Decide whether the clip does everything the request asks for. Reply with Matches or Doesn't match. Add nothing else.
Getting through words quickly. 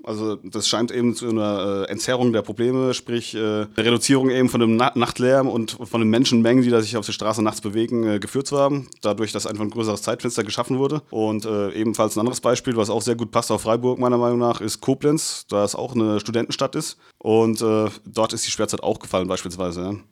Matches